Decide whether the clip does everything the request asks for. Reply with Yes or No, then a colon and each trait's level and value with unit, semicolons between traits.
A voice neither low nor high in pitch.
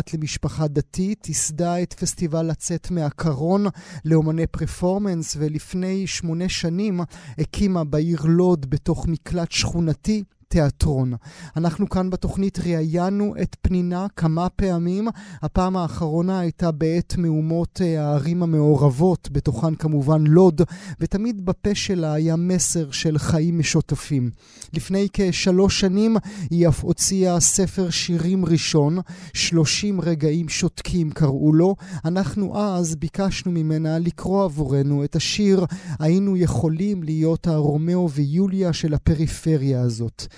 Yes: medium, 170 Hz